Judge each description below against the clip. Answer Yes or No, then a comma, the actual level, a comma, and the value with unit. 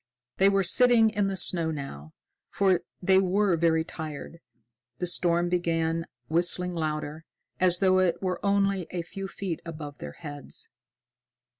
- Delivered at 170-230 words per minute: No, average, 145 wpm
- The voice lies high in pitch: No, medium, 175 Hz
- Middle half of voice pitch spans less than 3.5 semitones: Yes, average, 3.0 semitones